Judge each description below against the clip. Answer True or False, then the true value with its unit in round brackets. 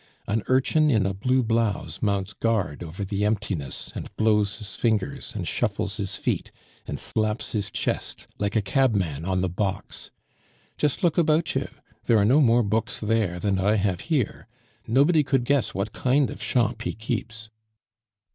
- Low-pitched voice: True (110 Hz)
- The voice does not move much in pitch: False (3.9 semitones)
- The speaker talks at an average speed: True (170 wpm)